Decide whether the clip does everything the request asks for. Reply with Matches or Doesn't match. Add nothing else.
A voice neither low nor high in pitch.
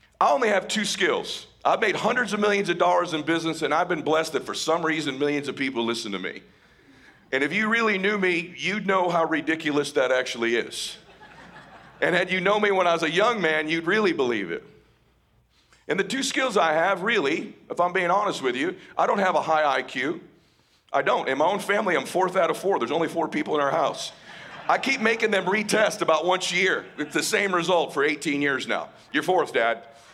Matches